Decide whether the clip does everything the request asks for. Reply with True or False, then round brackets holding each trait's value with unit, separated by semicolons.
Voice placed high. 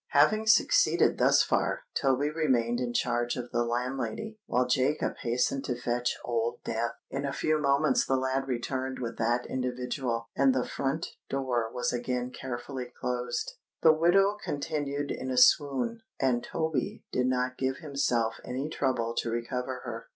False (130 Hz)